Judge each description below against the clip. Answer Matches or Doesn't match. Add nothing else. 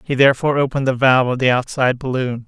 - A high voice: Doesn't match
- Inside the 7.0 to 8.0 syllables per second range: Matches